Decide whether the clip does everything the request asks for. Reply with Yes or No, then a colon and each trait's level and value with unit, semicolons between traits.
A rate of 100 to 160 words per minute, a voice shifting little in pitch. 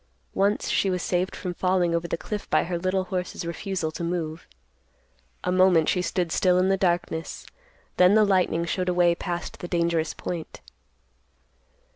No: average, 170 wpm; narrow, 1.6 semitones